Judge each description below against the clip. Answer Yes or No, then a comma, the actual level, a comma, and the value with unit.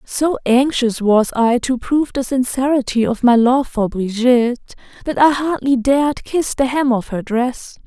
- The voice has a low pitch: No, very high, 255 Hz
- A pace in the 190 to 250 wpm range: No, average, 175 wpm